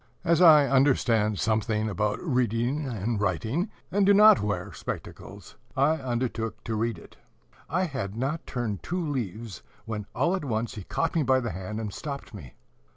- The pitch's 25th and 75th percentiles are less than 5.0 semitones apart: No, wide, 5.4 semitones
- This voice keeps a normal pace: Yes, average, 170 wpm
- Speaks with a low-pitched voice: Yes, low, 120 Hz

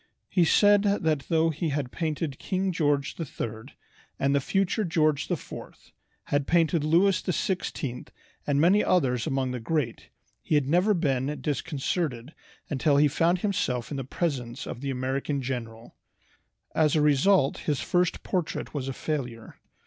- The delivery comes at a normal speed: Yes, average, 150 wpm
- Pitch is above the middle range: No, medium, 150 Hz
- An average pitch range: Yes, average, 4.3 semitones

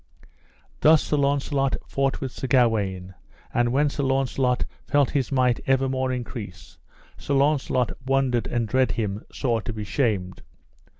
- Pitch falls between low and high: No, low, 130 Hz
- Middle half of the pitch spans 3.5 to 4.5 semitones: No, average, 2.9 semitones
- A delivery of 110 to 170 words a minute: Yes, average, 140 wpm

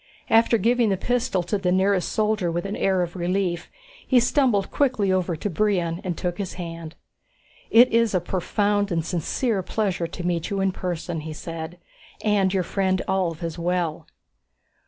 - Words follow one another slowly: No, average, 175 wpm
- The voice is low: No, medium, 185 Hz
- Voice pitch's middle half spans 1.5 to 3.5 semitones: Yes, average, 3.2 semitones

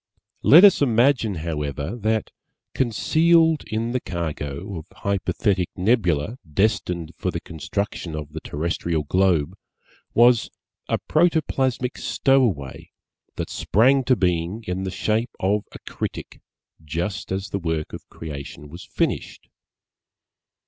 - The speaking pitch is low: Yes, very low, 95 Hz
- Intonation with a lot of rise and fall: Yes, wide, 6.5 semitones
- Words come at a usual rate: No, slow, 120 wpm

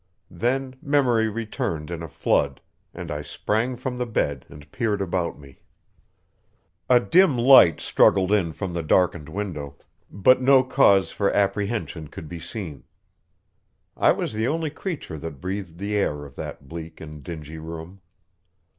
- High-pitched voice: No, very low, 95 Hz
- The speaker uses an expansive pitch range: Yes, wide, 6.7 semitones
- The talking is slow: No, average, 155 wpm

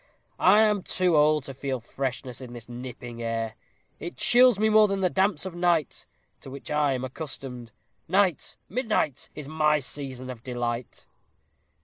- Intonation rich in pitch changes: Yes, wide, 6.6 semitones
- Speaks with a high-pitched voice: No, medium, 145 Hz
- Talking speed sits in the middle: Yes, average, 160 wpm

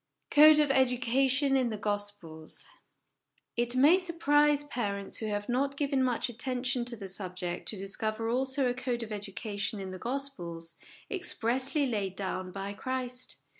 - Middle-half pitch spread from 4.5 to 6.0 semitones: Yes, average, 5.0 semitones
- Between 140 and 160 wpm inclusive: Yes, average, 150 wpm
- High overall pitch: Yes, high, 240 Hz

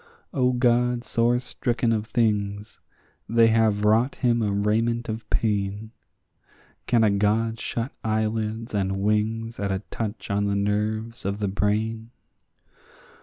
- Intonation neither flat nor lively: No, narrow, 2.0 semitones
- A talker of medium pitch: No, low, 110 Hz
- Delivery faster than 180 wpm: No, slow, 135 wpm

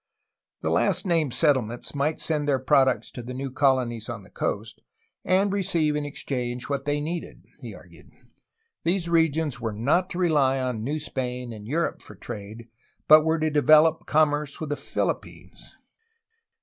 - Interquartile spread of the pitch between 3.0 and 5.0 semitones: Yes, average, 4.0 semitones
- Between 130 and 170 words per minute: Yes, average, 165 wpm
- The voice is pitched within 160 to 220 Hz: No, medium, 145 Hz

